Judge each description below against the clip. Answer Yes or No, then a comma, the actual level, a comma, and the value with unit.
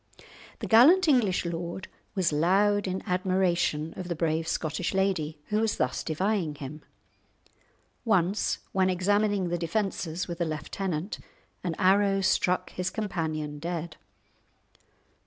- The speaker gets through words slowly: Yes, slow, 125 wpm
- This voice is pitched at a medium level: Yes, medium, 180 Hz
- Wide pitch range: No, average, 3.2 semitones